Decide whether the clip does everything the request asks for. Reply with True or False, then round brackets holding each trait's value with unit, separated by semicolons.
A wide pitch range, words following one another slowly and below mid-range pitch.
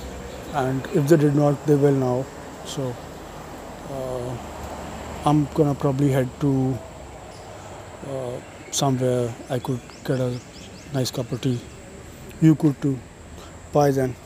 True (7.2 semitones; 125 wpm; 130 Hz)